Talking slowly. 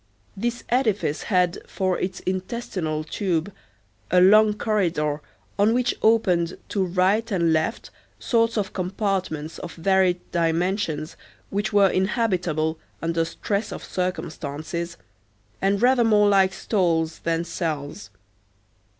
Yes: slow, 115 wpm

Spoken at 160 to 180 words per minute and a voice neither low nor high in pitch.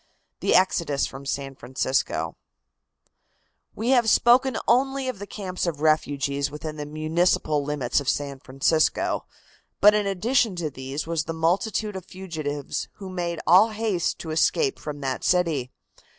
No: average, 150 wpm; medium, 165 Hz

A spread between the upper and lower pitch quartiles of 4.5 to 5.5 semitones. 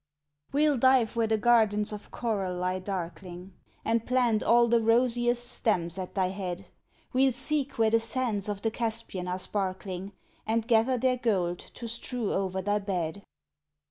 No: average, 4.1 semitones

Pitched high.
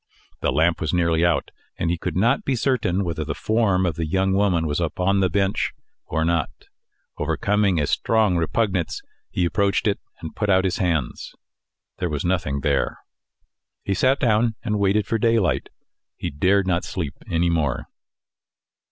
No: very low, 90 Hz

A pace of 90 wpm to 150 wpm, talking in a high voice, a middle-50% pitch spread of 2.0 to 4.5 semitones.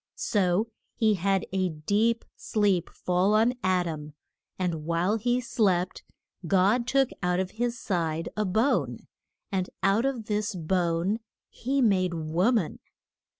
Yes: average, 145 wpm; high, 195 Hz; average, 4.0 semitones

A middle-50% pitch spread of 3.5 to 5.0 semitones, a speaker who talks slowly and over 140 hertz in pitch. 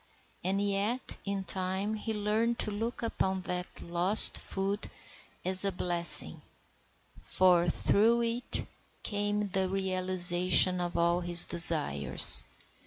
No: narrow, 2.5 semitones; slow, 115 wpm; high, 190 Hz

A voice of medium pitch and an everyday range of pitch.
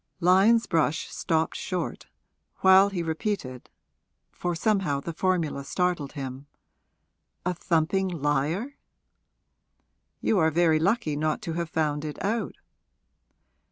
Yes: medium, 170 Hz; average, 3.7 semitones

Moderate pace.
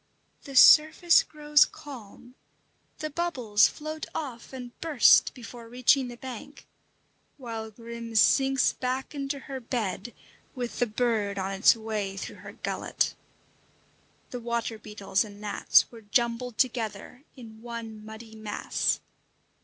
No: slow, 130 wpm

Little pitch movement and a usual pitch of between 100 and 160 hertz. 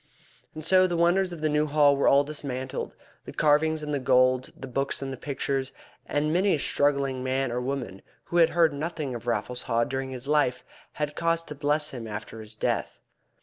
No: average, 3.0 semitones; medium, 140 Hz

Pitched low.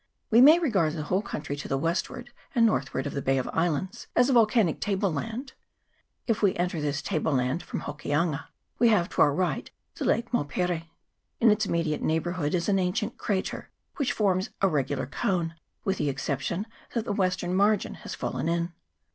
No: medium, 180 Hz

